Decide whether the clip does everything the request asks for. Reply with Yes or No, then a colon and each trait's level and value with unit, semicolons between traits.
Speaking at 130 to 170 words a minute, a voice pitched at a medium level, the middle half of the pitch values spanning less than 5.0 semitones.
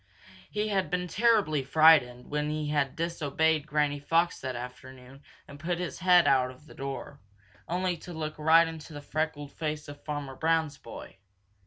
Yes: average, 165 wpm; medium, 150 Hz; average, 2.9 semitones